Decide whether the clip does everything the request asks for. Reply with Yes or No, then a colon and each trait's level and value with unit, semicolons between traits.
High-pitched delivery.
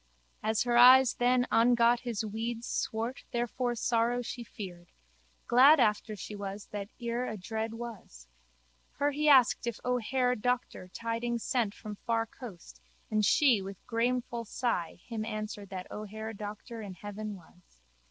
Yes: high, 230 Hz